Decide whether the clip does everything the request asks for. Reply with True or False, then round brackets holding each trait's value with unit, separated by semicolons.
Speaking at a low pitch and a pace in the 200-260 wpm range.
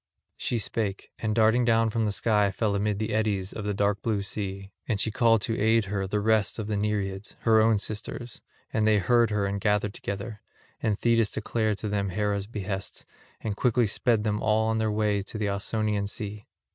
True (105 Hz; 205 wpm)